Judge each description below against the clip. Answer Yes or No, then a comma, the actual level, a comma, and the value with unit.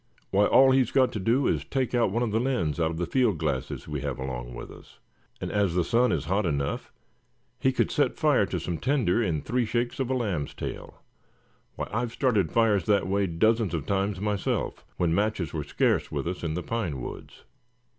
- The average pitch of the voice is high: No, low, 100 Hz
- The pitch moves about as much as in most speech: No, wide, 6.0 semitones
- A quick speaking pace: Yes, fast, 215 wpm